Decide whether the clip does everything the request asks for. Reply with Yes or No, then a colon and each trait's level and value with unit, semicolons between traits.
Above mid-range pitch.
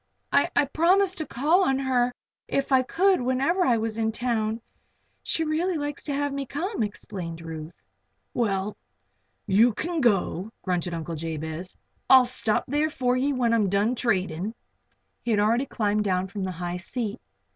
Yes: high, 235 Hz